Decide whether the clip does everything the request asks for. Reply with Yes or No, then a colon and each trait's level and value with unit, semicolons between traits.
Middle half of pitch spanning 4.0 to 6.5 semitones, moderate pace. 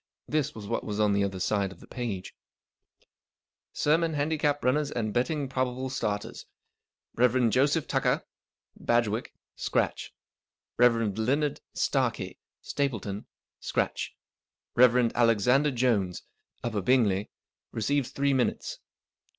No: average, 4.6 semitones; slow, 115 wpm